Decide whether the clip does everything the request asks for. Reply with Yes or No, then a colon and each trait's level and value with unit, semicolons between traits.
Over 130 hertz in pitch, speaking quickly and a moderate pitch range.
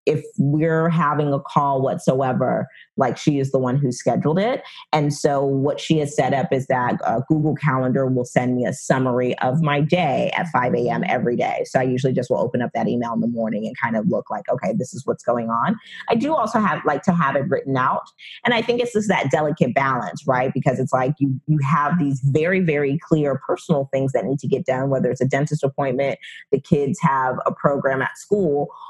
Yes: medium, 140 Hz; fast, 230 wpm; average, 3.3 semitones